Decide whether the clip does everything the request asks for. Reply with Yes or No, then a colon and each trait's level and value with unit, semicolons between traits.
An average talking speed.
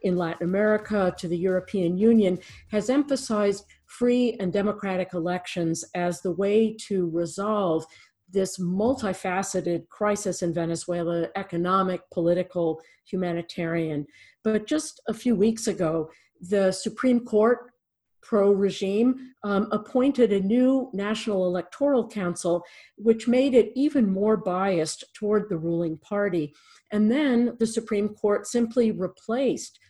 No: slow, 120 wpm